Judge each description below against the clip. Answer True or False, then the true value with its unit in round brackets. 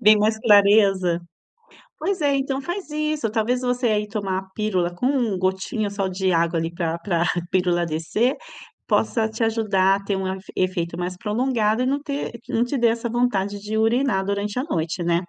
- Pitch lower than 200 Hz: False (210 Hz)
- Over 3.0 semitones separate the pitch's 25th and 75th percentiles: True (4.4 semitones)